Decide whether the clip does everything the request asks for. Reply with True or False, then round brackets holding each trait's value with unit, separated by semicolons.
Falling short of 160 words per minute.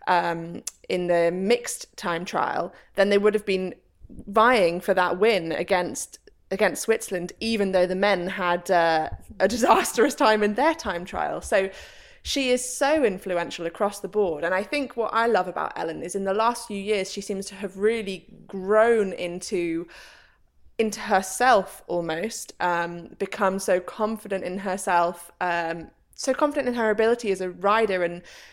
False (165 wpm)